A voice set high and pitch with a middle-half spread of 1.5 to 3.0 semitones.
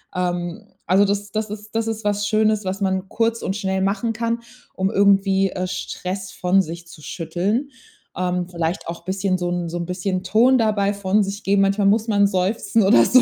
Yes: high, 195 Hz; narrow, 2.5 semitones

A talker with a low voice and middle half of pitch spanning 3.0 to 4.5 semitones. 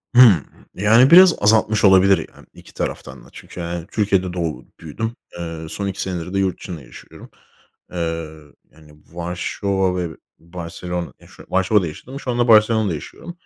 Yes: very low, 90 Hz; average, 4.0 semitones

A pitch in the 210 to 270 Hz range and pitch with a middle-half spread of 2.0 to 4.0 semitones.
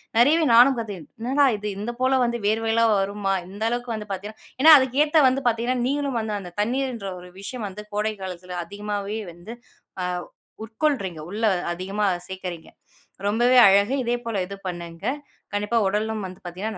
Yes: high, 215 Hz; average, 3.5 semitones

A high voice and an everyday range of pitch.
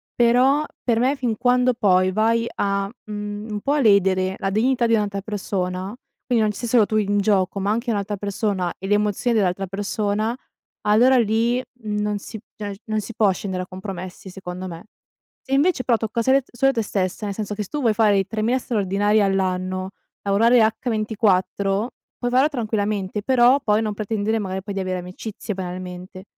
Yes: high, 210 Hz; average, 3.0 semitones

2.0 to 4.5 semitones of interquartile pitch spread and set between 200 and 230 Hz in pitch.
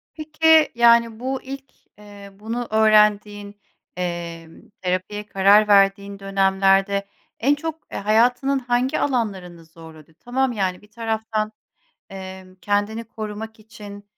Yes: average, 3.1 semitones; high, 210 Hz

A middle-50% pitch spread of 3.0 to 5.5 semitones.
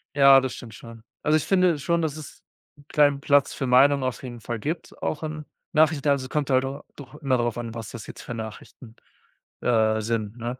Yes: average, 3.8 semitones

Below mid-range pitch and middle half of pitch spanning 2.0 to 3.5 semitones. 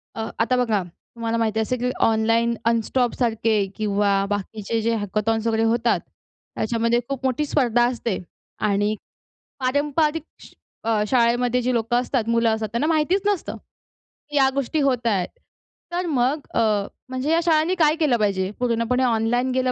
No: high, 235 Hz; average, 2.9 semitones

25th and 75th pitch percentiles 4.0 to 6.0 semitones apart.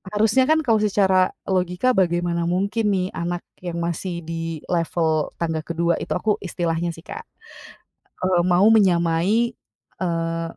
No: average, 2.9 semitones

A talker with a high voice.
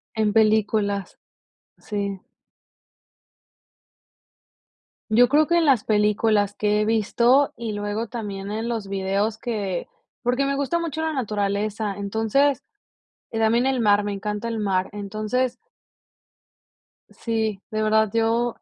Yes: high, 220 Hz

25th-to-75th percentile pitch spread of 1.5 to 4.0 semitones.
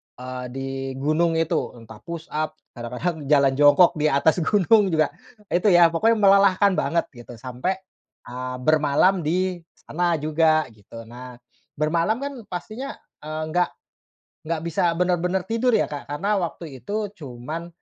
No: average, 4.6 semitones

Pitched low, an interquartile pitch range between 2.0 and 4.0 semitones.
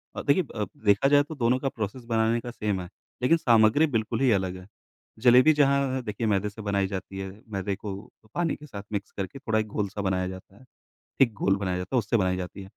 No: low, 105 Hz; average, 4.7 semitones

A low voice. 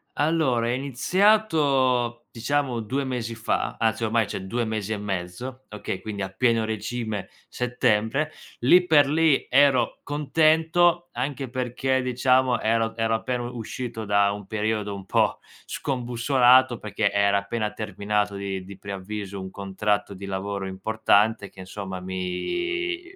Yes: low, 115 Hz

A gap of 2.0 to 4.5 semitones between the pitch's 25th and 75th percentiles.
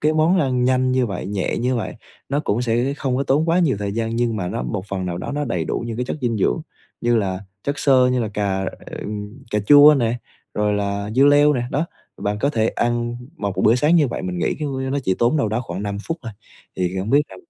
No: average, 5.2 semitones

